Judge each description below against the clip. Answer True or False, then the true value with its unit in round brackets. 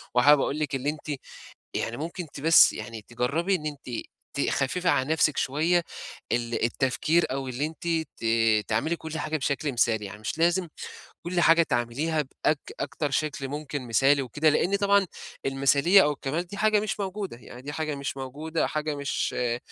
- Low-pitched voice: False (145 Hz)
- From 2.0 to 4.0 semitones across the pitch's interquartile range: True (3.7 semitones)